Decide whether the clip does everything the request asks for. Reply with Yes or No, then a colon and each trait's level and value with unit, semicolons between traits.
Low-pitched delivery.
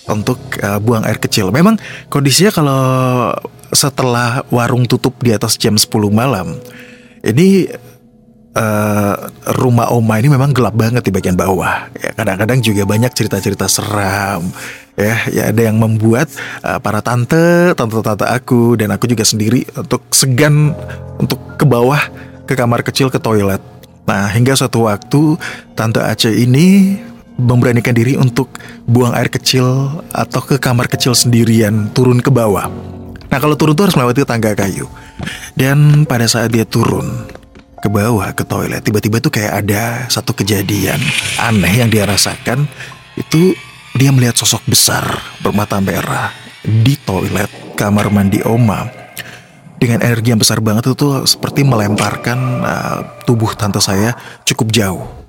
Yes: low, 120 Hz